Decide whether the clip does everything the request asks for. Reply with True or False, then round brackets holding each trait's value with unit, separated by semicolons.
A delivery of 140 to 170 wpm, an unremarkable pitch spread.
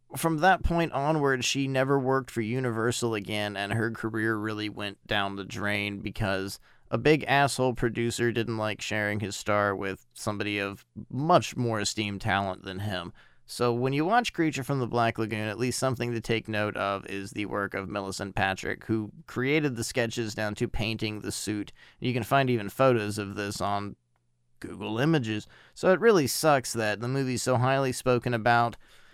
False (185 wpm; 3.8 semitones)